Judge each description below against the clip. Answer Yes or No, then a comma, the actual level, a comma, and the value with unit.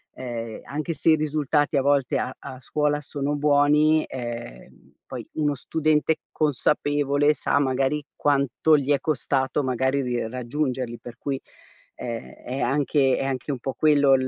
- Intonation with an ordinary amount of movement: No, narrow, 2.3 semitones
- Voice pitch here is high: No, medium, 140 Hz